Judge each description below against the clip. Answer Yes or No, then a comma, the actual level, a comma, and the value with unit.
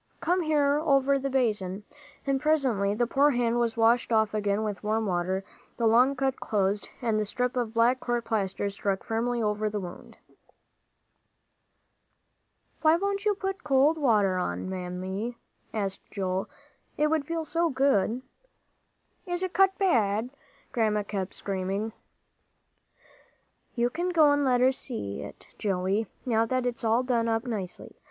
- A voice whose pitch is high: Yes, high, 230 Hz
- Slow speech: No, average, 150 wpm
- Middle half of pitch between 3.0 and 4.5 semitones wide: No, average, 5.1 semitones